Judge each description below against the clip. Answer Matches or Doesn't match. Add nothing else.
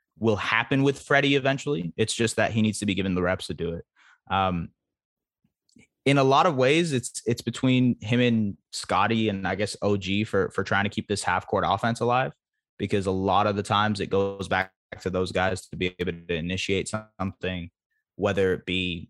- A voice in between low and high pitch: Doesn't match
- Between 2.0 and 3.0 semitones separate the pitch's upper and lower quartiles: Doesn't match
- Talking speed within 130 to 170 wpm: Doesn't match